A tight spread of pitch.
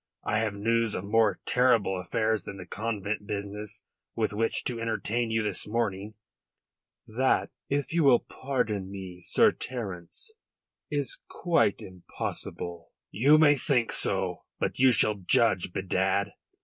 No: average, 3.1 semitones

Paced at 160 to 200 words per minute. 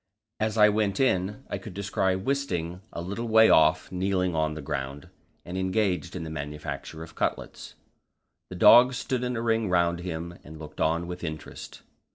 Yes: average, 180 wpm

